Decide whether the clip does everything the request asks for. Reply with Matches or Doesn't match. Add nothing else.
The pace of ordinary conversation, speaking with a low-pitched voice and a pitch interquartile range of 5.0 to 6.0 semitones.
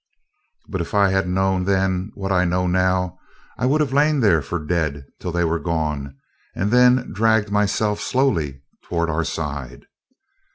Doesn't match